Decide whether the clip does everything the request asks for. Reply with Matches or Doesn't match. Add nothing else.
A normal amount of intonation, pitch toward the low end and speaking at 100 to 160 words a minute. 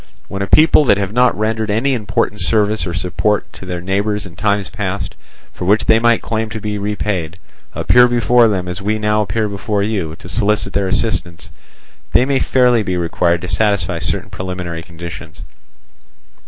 Doesn't match